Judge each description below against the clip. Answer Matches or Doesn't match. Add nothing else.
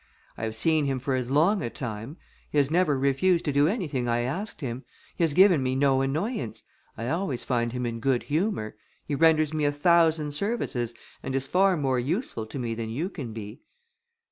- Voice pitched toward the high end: Doesn't match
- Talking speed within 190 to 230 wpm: Matches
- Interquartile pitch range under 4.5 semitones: Doesn't match